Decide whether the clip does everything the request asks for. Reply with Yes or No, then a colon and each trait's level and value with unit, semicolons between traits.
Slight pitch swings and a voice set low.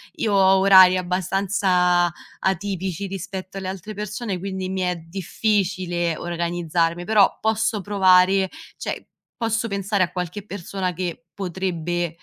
No: narrow, 2.1 semitones; medium, 185 Hz